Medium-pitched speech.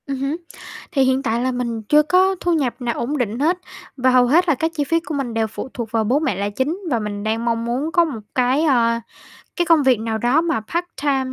No: very high, 260 Hz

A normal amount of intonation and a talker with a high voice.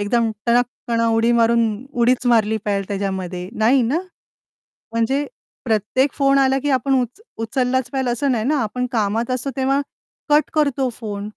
Yes: average, 3.2 semitones; high, 240 Hz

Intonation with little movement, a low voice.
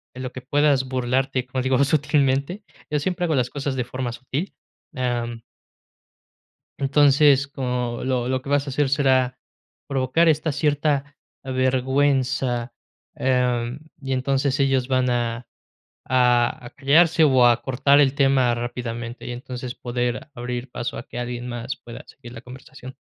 Yes: narrow, 2.2 semitones; low, 130 Hz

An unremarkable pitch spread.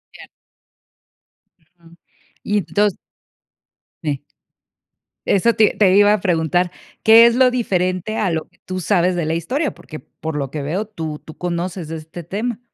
Yes: average, 4.2 semitones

